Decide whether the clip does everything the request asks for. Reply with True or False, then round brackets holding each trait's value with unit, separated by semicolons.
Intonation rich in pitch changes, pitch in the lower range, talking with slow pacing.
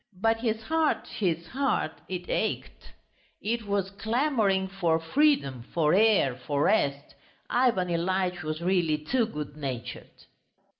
False (6.2 semitones; 185 Hz; 130 wpm)